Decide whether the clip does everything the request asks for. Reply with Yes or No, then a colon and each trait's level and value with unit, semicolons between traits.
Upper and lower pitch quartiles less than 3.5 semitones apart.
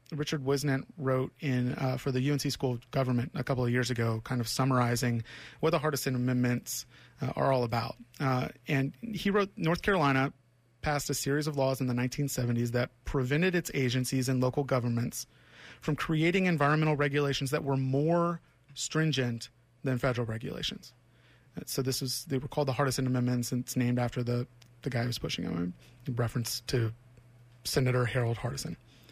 Yes: average, 2.7 semitones